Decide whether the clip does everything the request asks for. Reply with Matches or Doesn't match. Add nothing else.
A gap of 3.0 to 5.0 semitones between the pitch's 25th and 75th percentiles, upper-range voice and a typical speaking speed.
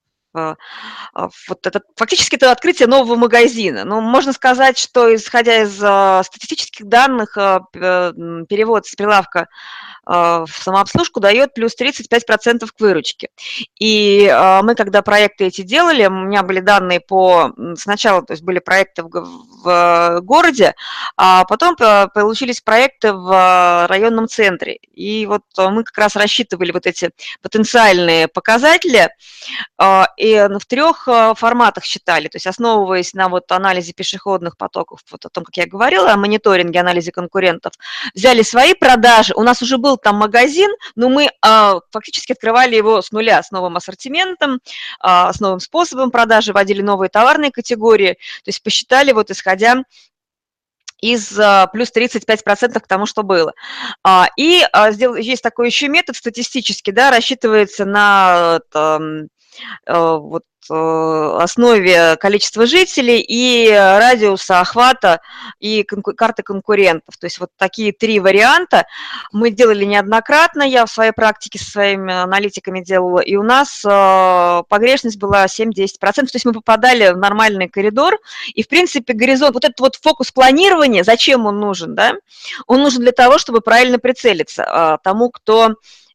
Matches